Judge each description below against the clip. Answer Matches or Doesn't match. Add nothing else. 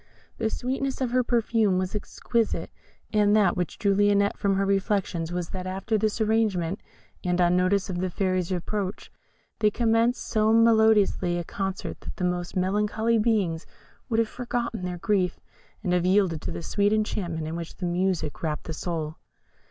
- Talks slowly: Doesn't match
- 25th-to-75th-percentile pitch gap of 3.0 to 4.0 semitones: Matches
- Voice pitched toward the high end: Matches